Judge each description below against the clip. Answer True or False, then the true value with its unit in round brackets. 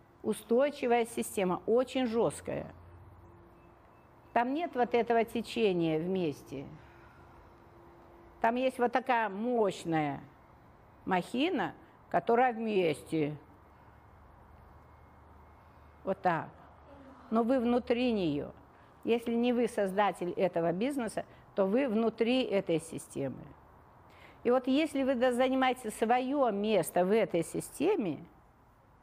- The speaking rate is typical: False (95 wpm)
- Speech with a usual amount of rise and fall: False (6.5 semitones)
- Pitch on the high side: True (220 Hz)